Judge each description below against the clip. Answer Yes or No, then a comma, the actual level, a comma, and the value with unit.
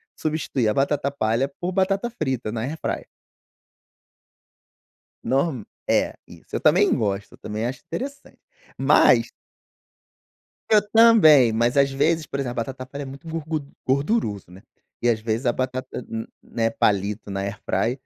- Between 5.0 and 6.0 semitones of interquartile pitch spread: Yes, wide, 5.6 semitones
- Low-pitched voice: Yes, low, 130 Hz